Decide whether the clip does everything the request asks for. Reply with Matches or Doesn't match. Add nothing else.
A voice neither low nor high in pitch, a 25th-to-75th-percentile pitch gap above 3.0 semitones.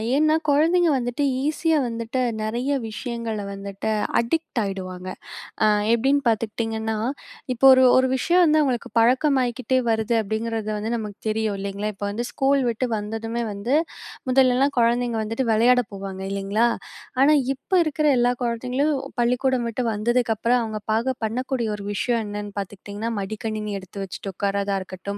Doesn't match